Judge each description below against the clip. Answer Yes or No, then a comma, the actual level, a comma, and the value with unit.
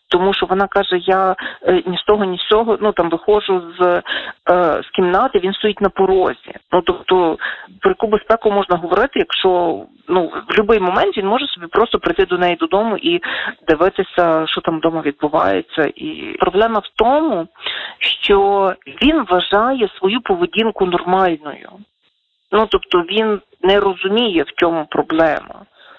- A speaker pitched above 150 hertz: Yes, high, 190 Hz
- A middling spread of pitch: Yes, average, 3.1 semitones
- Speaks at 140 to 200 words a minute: Yes, average, 150 wpm